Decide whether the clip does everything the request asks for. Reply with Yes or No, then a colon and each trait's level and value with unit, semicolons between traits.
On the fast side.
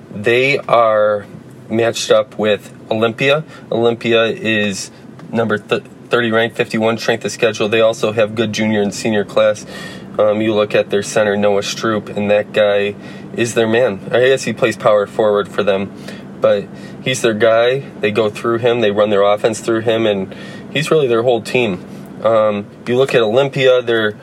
No: average, 180 wpm